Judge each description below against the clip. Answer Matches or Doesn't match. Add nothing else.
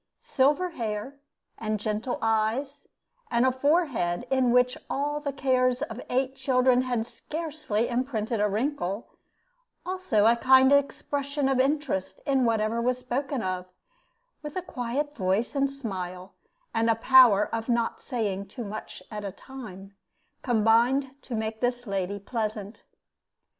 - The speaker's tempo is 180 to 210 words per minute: Doesn't match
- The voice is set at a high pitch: Matches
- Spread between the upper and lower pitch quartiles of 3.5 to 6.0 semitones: Matches